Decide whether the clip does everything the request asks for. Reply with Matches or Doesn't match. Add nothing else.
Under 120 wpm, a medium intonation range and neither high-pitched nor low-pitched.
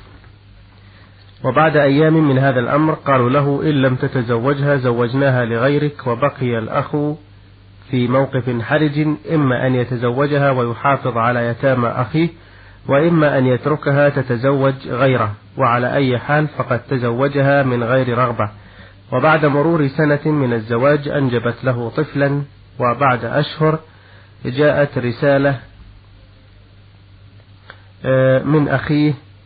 Doesn't match